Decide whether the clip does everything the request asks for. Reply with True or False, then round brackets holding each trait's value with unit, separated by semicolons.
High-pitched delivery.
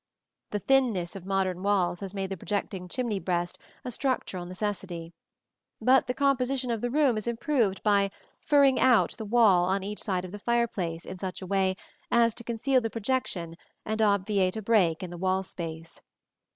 True (200 Hz)